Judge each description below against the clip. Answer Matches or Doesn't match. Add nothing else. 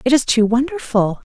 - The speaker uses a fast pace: Doesn't match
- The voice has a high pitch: Matches